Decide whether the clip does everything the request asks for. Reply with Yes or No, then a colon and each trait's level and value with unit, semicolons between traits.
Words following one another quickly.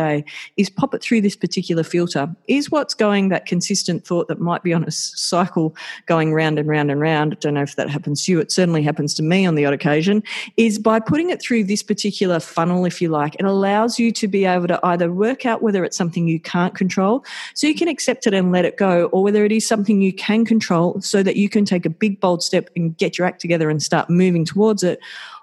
Yes: fast, 250 wpm